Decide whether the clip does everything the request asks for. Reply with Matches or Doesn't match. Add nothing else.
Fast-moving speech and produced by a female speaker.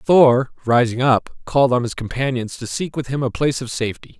Doesn't match